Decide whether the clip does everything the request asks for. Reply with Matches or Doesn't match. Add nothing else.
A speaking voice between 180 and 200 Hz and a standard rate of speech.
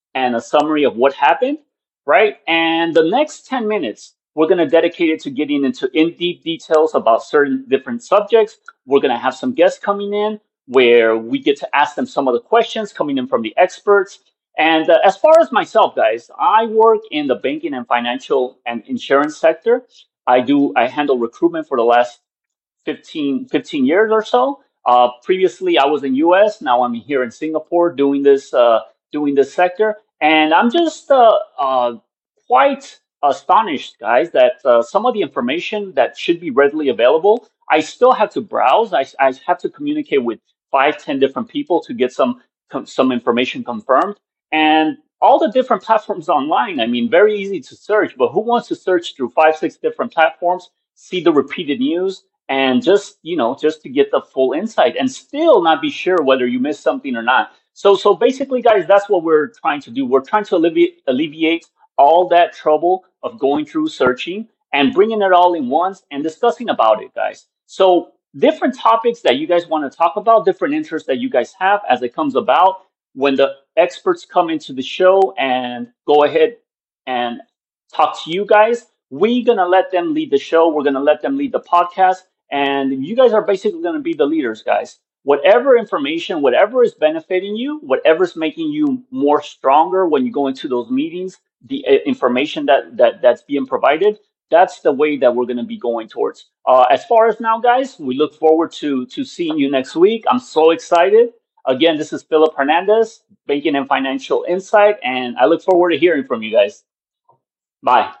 Matches